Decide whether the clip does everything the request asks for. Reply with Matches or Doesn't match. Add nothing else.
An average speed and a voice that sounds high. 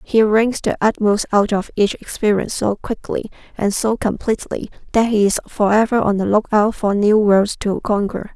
Matches